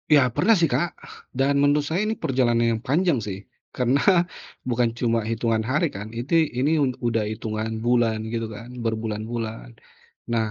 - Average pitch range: Yes, average, 3.9 semitones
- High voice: No, low, 120 Hz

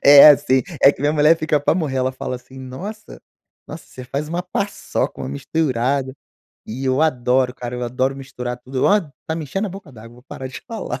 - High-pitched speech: No, low, 130 Hz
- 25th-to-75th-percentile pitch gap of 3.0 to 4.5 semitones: Yes, average, 3.7 semitones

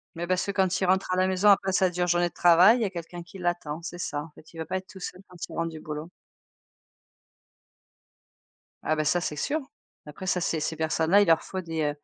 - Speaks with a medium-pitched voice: Yes, medium, 175 Hz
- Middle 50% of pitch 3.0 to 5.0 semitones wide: No, narrow, 2.6 semitones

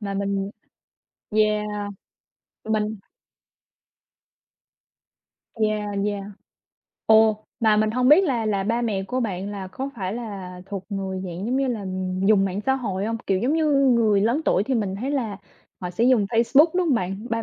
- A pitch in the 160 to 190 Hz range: No, high, 215 Hz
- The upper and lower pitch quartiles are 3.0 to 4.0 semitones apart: Yes, average, 3.3 semitones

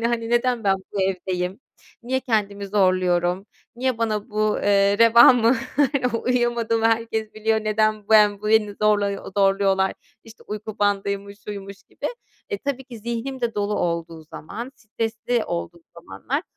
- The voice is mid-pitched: No, high, 215 Hz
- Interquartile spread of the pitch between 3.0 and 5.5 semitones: No, narrow, 2.6 semitones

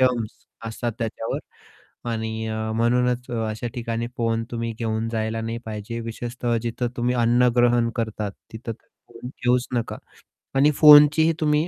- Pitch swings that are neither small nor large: No, narrow, 1.5 semitones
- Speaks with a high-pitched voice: No, low, 115 Hz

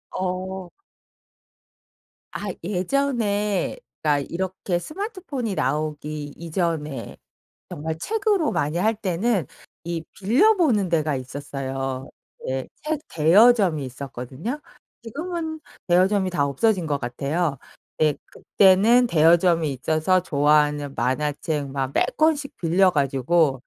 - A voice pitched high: No, medium, 170 Hz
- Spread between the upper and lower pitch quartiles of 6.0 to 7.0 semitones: Yes, wide, 6.3 semitones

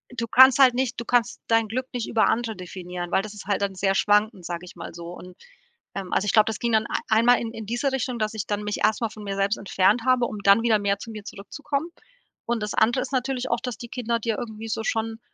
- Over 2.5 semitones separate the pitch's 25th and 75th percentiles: Yes, average, 2.9 semitones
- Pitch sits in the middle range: No, high, 220 Hz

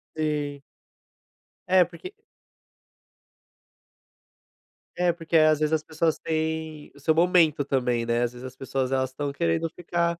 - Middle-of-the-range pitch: Yes, medium, 155 Hz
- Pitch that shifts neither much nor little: Yes, average, 3.6 semitones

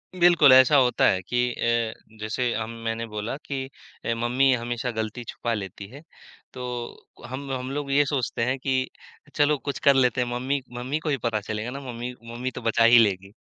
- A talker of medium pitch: No, low, 125 Hz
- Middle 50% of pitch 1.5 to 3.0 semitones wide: Yes, average, 2.7 semitones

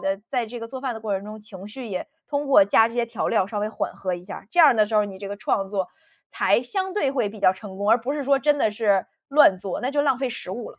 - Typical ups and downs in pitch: Yes, average, 4.9 semitones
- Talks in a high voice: Yes, high, 220 Hz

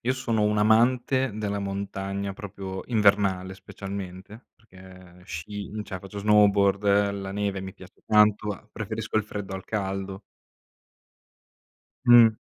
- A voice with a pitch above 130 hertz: No, low, 100 Hz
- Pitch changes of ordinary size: No, narrow, 1.8 semitones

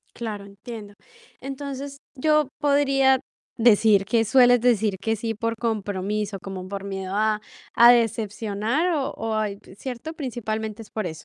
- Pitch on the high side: Yes, high, 225 Hz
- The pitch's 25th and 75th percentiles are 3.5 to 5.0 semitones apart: Yes, average, 3.8 semitones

